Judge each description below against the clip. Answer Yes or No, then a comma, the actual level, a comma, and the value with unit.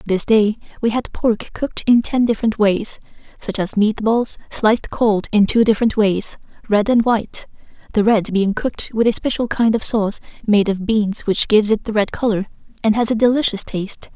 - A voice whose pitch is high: Yes, high, 215 Hz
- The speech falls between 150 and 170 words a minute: No, average, 200 wpm